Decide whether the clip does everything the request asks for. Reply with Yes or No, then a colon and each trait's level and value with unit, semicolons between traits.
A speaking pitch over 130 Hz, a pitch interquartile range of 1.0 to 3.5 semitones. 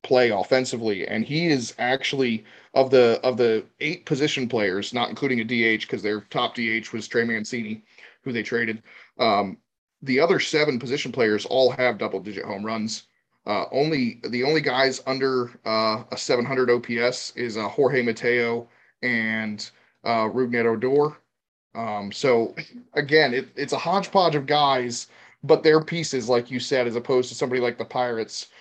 No: low, 125 Hz; average, 2.8 semitones